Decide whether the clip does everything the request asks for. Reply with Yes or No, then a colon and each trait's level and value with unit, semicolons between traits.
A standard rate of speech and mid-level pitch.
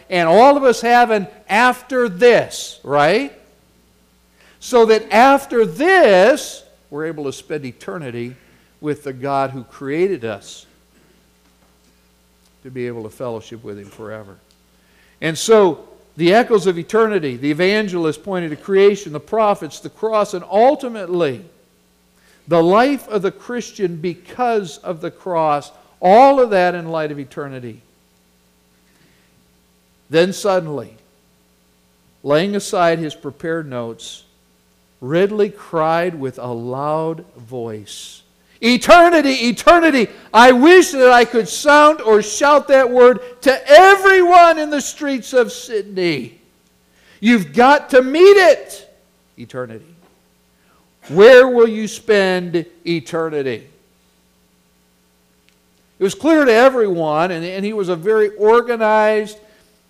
No: slow, 120 wpm; medium, 170 Hz